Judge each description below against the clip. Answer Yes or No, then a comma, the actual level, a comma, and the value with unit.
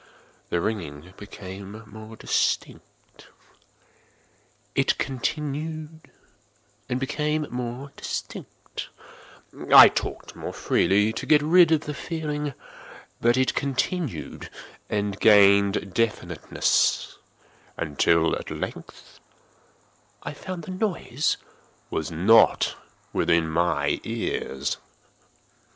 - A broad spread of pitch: Yes, wide, 7.4 semitones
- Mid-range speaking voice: No, low, 115 Hz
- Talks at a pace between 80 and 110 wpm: Yes, slow, 90 wpm